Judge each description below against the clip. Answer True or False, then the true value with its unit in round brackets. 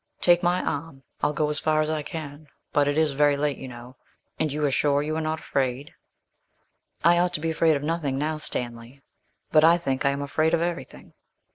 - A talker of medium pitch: True (150 Hz)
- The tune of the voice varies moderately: False (2.3 semitones)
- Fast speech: True (220 wpm)